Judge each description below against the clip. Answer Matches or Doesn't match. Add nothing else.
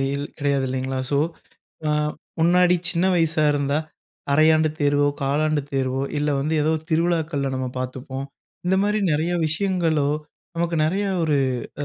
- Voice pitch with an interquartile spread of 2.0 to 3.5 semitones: Matches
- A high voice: Doesn't match